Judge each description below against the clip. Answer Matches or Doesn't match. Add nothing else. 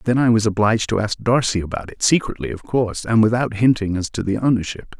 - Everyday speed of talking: Doesn't match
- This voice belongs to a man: Matches